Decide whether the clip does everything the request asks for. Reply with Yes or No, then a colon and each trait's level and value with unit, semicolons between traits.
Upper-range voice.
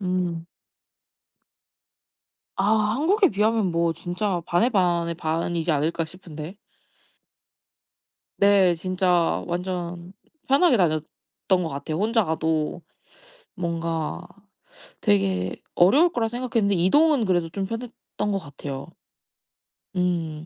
No: medium, 175 Hz